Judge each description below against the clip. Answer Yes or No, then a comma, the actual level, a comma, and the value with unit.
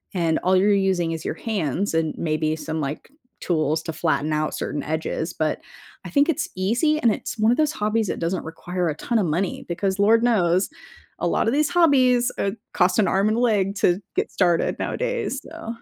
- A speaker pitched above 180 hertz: Yes, high, 190 Hz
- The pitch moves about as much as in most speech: No, wide, 5.8 semitones